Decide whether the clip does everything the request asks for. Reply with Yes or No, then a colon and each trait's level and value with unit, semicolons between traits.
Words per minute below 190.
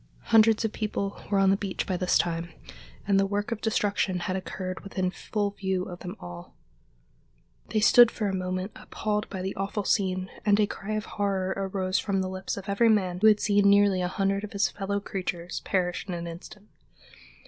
No: fast, 205 wpm